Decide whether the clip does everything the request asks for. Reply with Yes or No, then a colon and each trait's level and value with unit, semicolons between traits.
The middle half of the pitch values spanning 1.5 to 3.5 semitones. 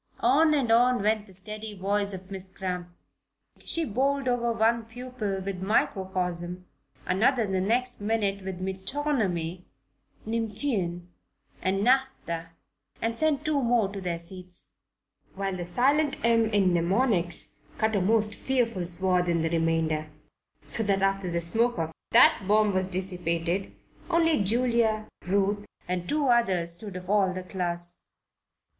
No: average, 4.3 semitones